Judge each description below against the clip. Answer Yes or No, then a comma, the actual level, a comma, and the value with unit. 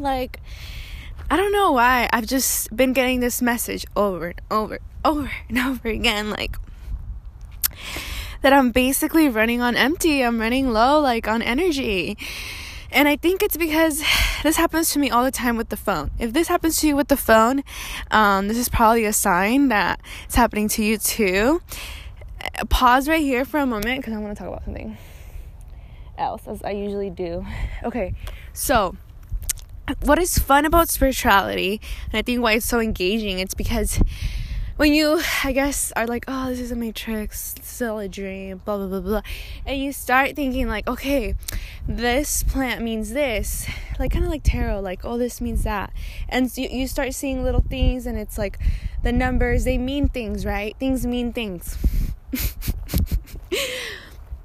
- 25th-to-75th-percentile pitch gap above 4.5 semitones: Yes, average, 5.0 semitones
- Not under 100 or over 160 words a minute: No, average, 175 wpm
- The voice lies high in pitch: Yes, high, 240 Hz